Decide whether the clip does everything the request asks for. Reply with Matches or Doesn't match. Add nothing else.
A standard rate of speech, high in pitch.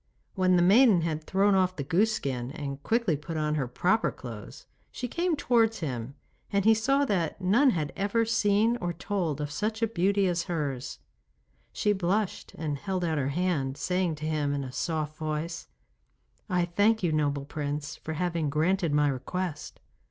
Doesn't match